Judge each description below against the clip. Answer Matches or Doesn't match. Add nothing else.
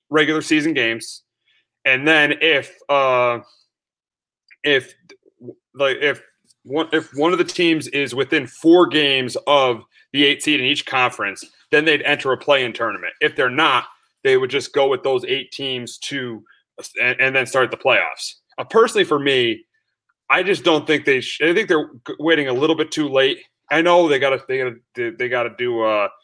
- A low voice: Doesn't match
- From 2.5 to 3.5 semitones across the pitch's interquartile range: Doesn't match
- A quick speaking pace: Doesn't match